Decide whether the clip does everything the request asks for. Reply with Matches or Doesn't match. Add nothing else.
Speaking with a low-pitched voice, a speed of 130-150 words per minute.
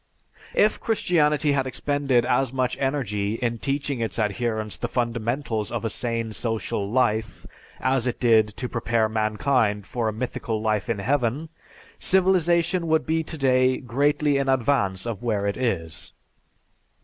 Matches